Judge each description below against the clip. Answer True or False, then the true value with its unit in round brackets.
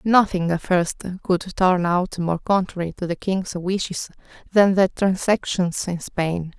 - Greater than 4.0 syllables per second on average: False (3.9 syllables/s)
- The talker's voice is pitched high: False (180 Hz)